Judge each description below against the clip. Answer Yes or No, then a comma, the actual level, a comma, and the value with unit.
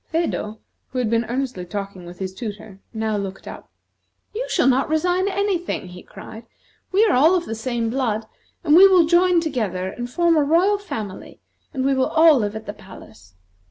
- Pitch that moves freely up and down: Yes, wide, 8.2 semitones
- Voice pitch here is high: Yes, very high, 250 Hz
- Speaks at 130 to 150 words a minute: No, average, 195 wpm